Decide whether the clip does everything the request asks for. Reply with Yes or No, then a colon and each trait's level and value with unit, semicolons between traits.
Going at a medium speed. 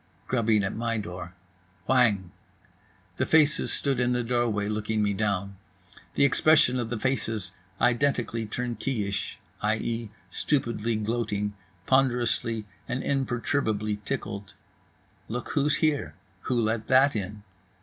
No: slow, 120 wpm